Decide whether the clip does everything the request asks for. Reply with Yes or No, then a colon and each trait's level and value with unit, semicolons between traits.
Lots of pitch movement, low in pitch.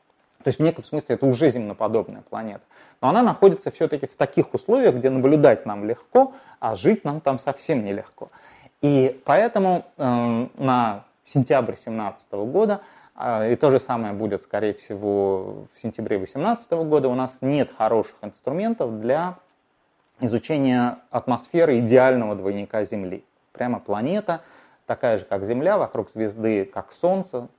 Yes: wide, 6.3 semitones; low, 130 Hz